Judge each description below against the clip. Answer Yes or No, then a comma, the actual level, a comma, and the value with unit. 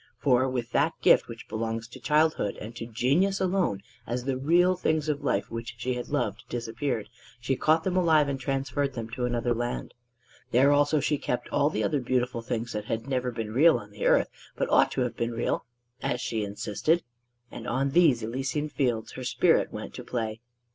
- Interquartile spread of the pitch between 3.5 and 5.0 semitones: Yes, average, 3.8 semitones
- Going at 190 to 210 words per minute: Yes, average, 200 wpm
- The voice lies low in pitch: Yes, low, 125 Hz